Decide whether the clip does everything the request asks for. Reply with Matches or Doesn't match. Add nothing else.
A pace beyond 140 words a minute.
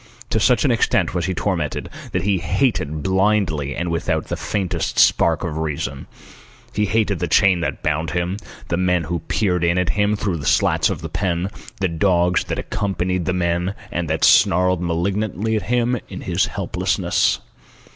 Matches